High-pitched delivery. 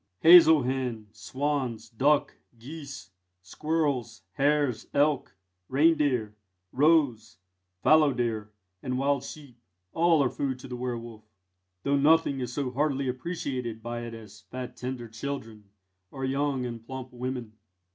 No: low, 130 Hz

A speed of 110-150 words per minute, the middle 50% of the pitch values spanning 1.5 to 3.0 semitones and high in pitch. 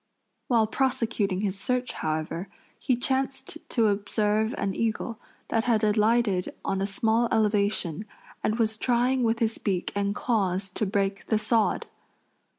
Yes: average, 145 wpm; average, 2.7 semitones; high, 215 Hz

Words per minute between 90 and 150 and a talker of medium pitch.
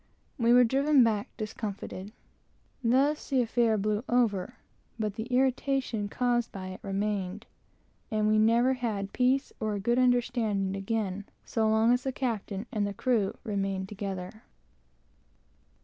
No: slow, 135 wpm; high, 220 Hz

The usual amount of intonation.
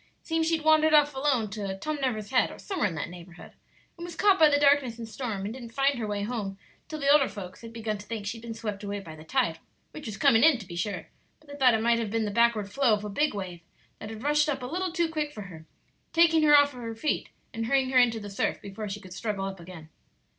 No: wide, 6.1 semitones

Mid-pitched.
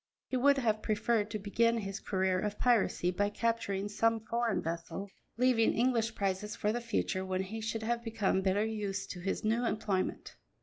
No: high, 215 Hz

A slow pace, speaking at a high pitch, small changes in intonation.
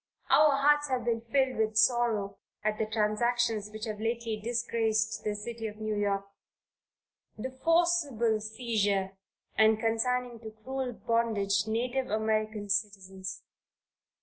Yes: slow, 125 wpm; high, 220 Hz; narrow, 2.2 semitones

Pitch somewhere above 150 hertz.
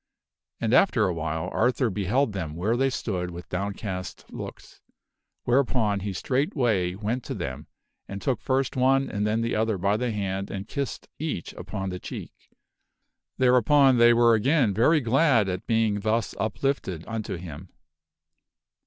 No: low, 110 Hz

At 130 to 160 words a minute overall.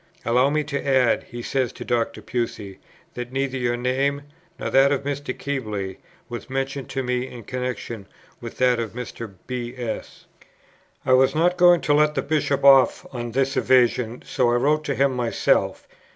No: average, 180 wpm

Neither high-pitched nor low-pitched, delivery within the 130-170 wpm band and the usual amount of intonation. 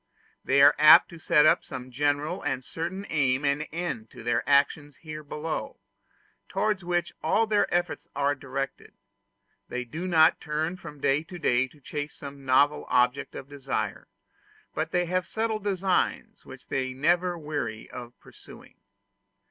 Yes: medium, 150 Hz; average, 160 wpm; average, 4.3 semitones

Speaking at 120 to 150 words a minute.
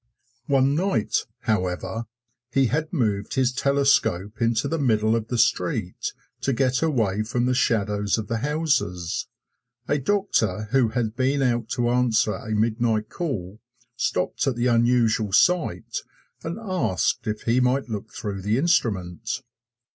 Yes: average, 145 wpm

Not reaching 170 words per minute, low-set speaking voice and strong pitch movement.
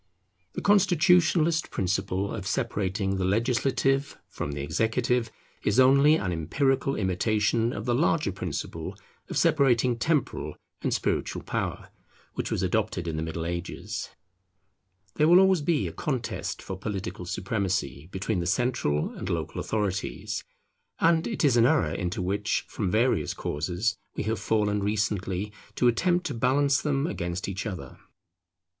Yes: average, 145 wpm; low, 110 Hz; wide, 6.5 semitones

